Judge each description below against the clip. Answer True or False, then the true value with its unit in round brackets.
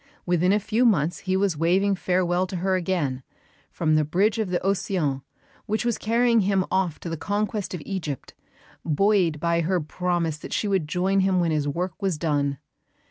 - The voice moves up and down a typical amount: True (3.3 semitones)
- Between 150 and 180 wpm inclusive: False (190 wpm)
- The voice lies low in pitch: False (180 Hz)